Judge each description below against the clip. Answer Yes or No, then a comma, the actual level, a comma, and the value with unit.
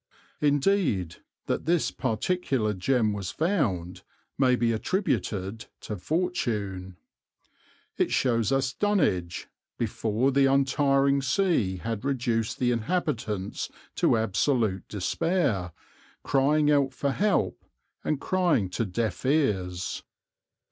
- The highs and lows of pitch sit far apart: Yes, wide, 5.9 semitones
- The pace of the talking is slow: Yes, slow, 105 wpm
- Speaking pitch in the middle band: No, low, 125 Hz